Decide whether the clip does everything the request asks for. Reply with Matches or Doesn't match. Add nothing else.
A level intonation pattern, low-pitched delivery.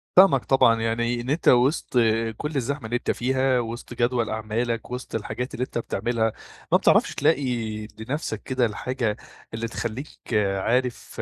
Matches